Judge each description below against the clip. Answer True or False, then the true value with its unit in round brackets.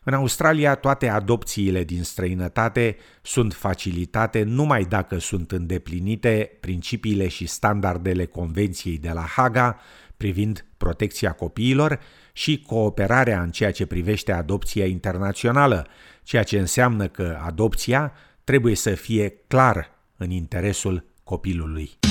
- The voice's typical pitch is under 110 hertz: True (100 Hz)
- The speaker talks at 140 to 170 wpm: False (115 wpm)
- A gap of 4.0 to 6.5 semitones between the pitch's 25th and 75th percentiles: True (4.6 semitones)